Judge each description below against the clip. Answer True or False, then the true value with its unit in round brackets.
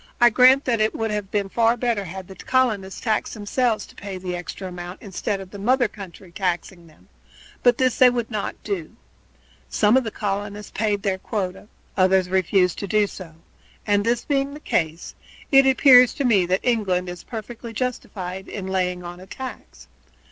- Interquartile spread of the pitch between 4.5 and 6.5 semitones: False (4.1 semitones)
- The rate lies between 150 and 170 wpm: False (185 wpm)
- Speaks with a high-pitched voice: True (205 Hz)